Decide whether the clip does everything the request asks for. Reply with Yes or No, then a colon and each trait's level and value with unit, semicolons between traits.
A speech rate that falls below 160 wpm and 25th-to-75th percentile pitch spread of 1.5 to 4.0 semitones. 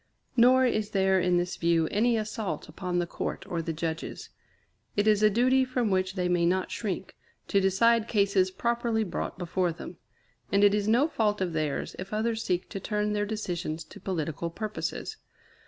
No: average, 185 wpm; average, 3.6 semitones